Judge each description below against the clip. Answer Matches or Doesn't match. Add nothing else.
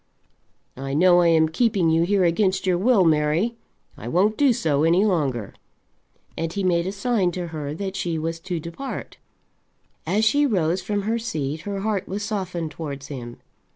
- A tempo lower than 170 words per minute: Doesn't match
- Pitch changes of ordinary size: Matches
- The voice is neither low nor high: Matches